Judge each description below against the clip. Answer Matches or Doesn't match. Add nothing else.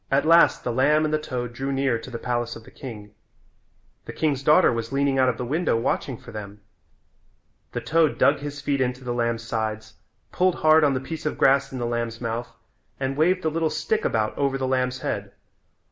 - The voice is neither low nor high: Doesn't match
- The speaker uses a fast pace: Matches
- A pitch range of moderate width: Matches